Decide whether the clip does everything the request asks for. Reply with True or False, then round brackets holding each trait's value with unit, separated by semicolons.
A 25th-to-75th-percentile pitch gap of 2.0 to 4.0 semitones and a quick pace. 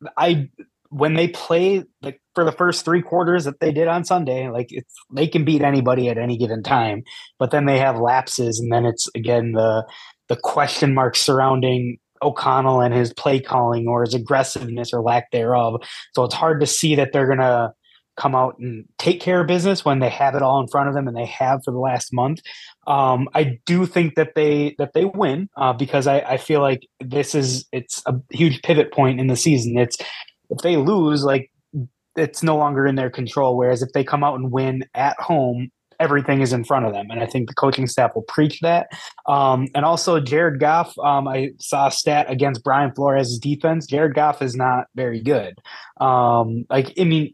True (3.1 semitones; 210 wpm)